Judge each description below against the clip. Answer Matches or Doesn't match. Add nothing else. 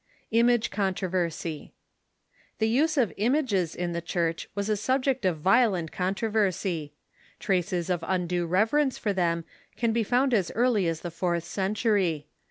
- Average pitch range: Matches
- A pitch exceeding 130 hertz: Matches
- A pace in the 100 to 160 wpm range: Matches